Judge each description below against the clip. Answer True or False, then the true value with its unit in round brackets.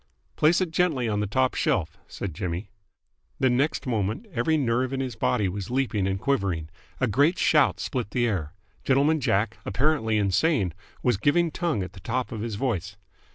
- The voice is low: True (120 Hz)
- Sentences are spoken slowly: False (180 wpm)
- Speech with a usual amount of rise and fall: False (5.7 semitones)